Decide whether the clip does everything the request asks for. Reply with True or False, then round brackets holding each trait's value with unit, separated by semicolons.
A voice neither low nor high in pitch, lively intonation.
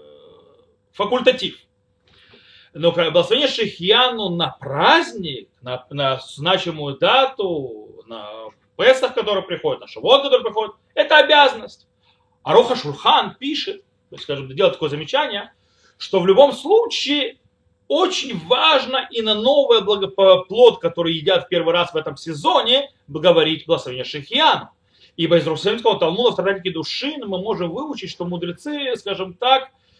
False (220 Hz; 8.9 semitones)